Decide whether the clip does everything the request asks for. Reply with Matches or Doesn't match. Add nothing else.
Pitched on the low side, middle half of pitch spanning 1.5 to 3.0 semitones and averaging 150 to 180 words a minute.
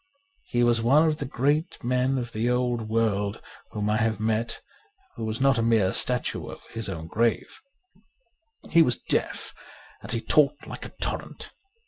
Matches